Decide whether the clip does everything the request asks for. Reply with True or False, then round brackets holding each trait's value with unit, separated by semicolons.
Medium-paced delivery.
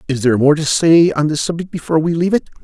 False (275 wpm)